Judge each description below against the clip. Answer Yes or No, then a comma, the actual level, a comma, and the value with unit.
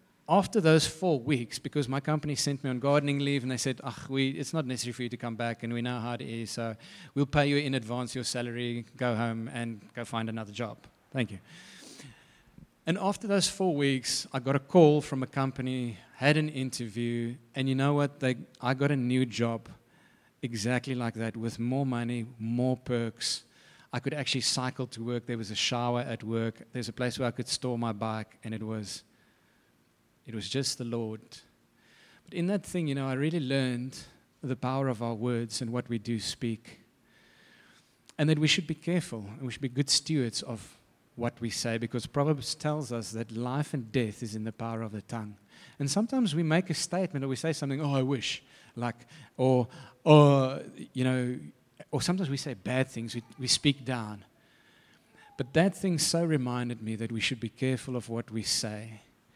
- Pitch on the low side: Yes, low, 125 Hz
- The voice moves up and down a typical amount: Yes, average, 3.4 semitones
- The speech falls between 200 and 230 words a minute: Yes, fast, 205 wpm